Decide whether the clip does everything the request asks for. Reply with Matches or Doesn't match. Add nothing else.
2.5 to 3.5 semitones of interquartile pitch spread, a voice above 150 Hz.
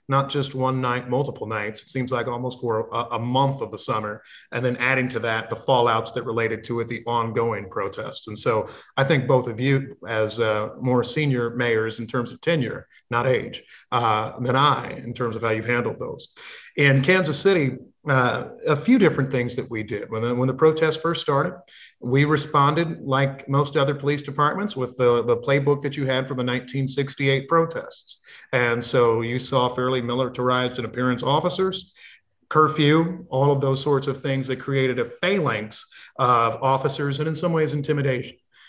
Doesn't match